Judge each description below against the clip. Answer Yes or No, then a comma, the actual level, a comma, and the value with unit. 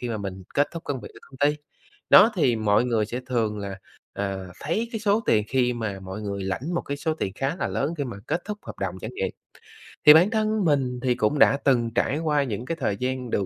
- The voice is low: Yes, low, 125 Hz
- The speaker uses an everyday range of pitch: No, wide, 6.5 semitones